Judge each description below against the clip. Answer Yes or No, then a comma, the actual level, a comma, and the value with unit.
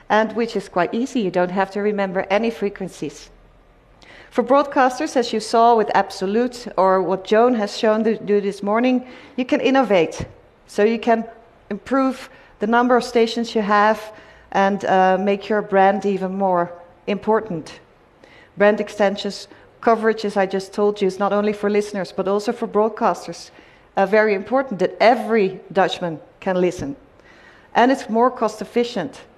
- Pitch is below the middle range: No, high, 210 Hz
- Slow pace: No, average, 160 wpm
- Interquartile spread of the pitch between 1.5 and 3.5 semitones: Yes, average, 2.9 semitones